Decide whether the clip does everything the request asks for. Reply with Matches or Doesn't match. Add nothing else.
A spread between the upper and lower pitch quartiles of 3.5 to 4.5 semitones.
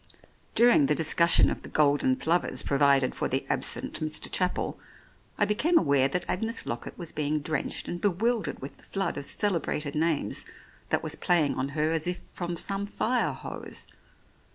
Doesn't match